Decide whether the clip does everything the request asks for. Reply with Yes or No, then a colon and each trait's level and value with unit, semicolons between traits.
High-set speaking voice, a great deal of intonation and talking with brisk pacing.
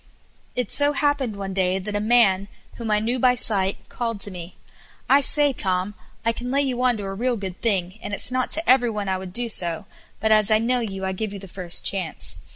No: high, 210 Hz; average, 4.3 semitones; fast, 240 wpm